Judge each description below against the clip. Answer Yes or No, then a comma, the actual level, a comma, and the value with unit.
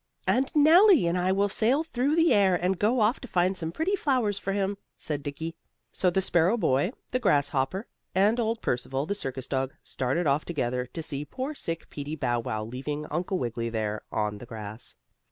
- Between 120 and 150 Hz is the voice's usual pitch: No, medium, 175 Hz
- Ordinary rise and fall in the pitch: No, wide, 8.1 semitones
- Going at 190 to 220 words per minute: Yes, average, 195 wpm